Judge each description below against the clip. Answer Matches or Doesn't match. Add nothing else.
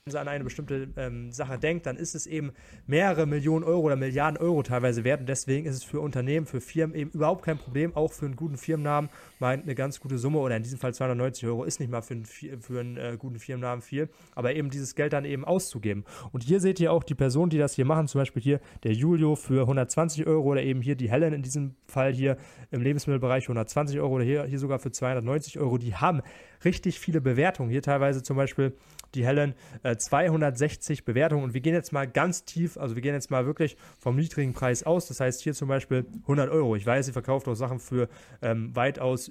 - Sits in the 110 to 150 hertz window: Matches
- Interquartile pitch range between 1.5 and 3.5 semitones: Matches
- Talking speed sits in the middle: Doesn't match